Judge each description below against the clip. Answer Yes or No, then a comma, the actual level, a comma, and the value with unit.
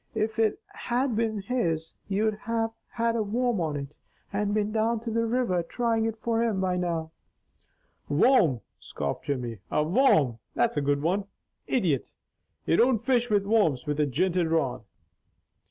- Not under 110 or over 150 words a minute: No, average, 165 wpm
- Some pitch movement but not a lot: No, wide, 6.3 semitones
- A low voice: No, high, 205 Hz